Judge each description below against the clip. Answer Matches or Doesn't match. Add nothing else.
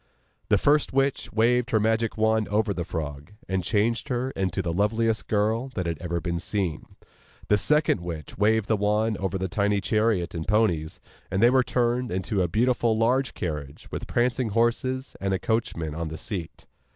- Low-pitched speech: Matches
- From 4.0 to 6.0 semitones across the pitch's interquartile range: Matches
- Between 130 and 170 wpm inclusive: Doesn't match